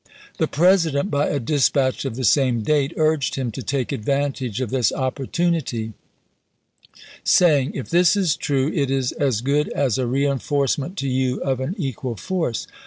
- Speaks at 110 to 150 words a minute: No, average, 170 wpm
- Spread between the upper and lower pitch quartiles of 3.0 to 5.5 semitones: No, narrow, 2.6 semitones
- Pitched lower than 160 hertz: Yes, low, 135 Hz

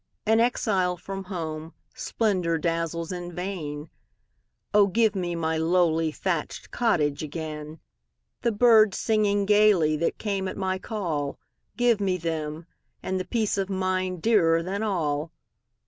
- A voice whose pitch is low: No, medium, 180 Hz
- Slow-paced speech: Yes, slow, 120 wpm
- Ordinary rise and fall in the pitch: Yes, average, 4.0 semitones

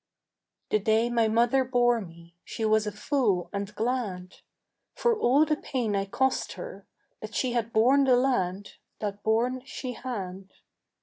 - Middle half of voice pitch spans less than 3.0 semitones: No, average, 4.1 semitones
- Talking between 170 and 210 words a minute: No, average, 160 wpm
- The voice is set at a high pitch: Yes, high, 230 Hz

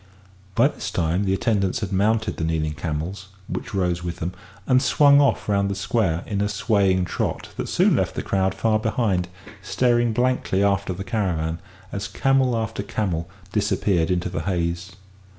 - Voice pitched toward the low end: Yes, low, 100 Hz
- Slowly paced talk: No, average, 175 wpm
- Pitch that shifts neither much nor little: Yes, average, 3.7 semitones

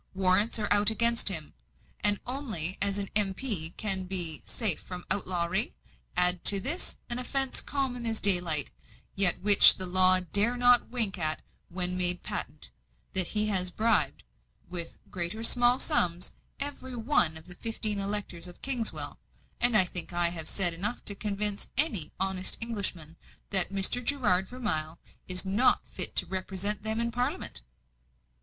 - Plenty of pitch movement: No, average, 4.2 semitones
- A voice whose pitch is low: No, high, 195 Hz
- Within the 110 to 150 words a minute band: No, average, 160 wpm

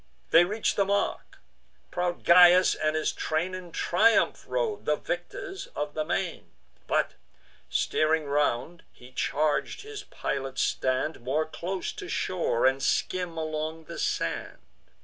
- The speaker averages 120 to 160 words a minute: Yes, slow, 135 wpm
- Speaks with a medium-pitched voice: Yes, medium, 165 Hz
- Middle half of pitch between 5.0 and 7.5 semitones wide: No, average, 3.3 semitones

